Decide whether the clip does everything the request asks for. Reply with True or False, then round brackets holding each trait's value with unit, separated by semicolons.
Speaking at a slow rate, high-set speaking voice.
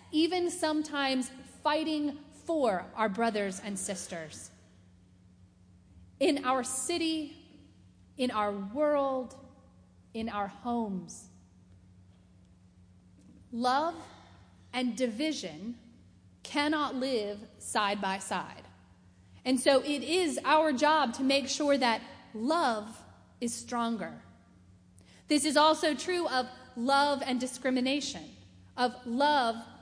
True (95 wpm; 235 Hz)